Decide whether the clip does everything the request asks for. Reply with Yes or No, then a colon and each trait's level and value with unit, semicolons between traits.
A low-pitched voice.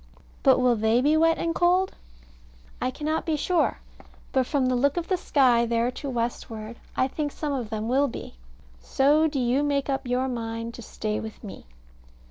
No: very high, 260 Hz